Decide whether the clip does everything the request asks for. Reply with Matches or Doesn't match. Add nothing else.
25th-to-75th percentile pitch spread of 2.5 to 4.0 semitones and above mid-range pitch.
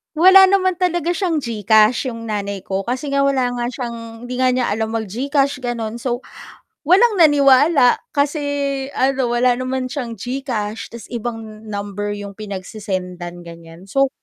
Doesn't match